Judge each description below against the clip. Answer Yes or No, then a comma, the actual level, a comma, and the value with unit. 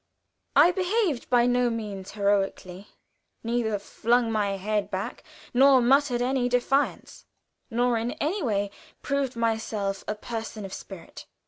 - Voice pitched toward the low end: No, high, 235 Hz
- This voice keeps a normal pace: No, slow, 130 wpm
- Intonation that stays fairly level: No, average, 3.4 semitones